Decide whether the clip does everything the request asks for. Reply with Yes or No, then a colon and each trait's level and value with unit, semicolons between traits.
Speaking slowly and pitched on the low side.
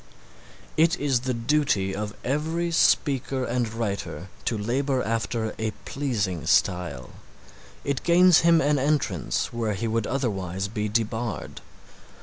Yes: slow, 130 wpm; low, 120 Hz